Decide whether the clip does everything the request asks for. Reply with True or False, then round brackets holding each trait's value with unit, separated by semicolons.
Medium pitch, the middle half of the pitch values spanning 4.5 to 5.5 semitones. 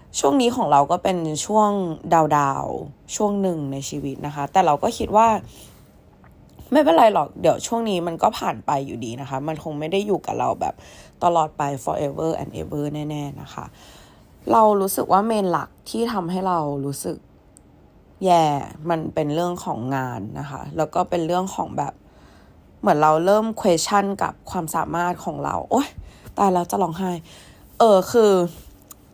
True (170 Hz; 5.0 semitones)